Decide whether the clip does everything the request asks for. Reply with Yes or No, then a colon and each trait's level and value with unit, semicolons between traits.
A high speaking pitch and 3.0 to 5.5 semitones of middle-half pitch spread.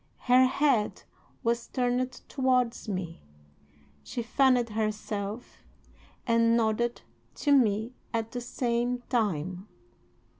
No: high, 235 Hz; narrow, 2.6 semitones